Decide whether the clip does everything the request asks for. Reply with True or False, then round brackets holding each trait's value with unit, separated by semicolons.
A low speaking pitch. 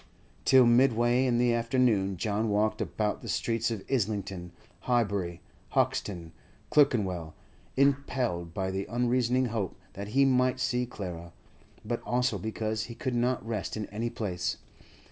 True (115 Hz)